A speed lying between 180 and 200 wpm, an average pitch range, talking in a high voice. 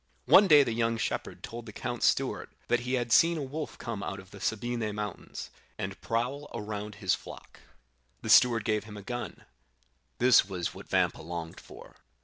No: average, 185 wpm; average, 3.0 semitones; low, 115 Hz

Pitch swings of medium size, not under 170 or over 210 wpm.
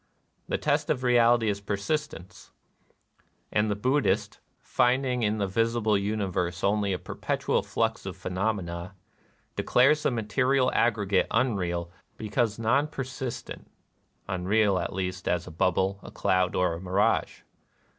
No: average, 4.6 semitones; slow, 135 wpm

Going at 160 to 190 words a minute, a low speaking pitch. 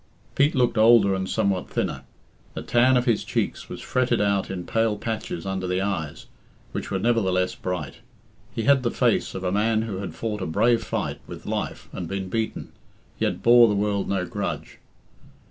Yes: average, 185 wpm; low, 105 Hz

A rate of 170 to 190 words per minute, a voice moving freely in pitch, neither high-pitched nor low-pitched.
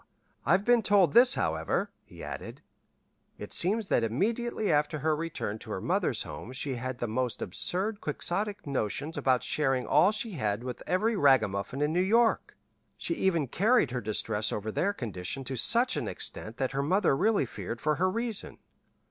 Yes: average, 175 wpm; wide, 8.3 semitones; medium, 150 Hz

